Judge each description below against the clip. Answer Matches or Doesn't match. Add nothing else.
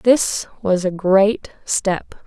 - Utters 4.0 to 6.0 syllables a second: Doesn't match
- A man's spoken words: Doesn't match